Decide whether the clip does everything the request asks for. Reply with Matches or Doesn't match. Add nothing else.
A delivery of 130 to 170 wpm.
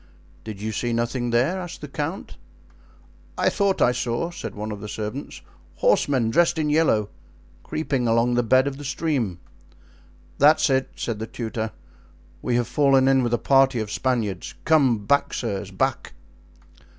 Matches